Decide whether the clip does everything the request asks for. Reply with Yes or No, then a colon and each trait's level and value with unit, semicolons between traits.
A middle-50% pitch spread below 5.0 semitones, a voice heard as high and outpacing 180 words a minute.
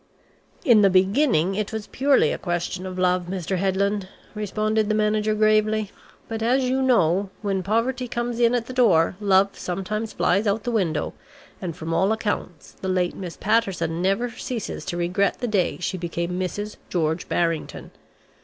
No: average, 3.4 semitones; high, 200 Hz; average, 175 wpm